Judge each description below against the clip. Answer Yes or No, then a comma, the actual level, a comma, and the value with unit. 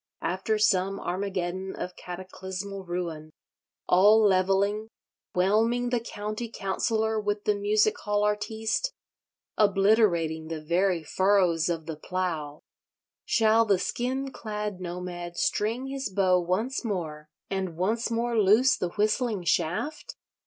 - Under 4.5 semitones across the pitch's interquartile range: Yes, average, 3.3 semitones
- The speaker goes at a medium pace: No, slow, 120 wpm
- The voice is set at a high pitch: Yes, high, 195 Hz